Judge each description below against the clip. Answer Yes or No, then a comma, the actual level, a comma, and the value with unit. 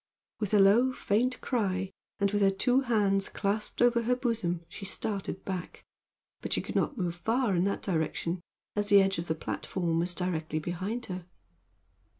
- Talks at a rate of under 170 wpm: No, average, 175 wpm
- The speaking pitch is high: Yes, high, 195 Hz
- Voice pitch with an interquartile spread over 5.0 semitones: No, average, 3.9 semitones